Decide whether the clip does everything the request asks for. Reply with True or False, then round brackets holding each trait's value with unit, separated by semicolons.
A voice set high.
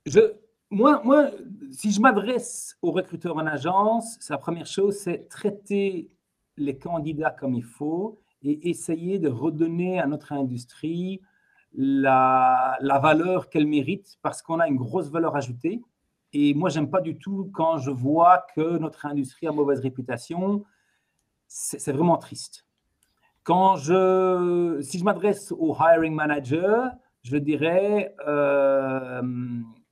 False (165 Hz)